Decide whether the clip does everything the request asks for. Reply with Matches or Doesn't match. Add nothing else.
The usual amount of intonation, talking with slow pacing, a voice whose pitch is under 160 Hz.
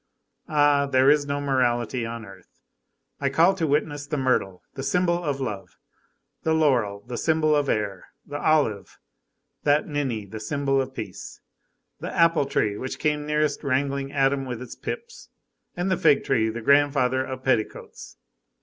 Doesn't match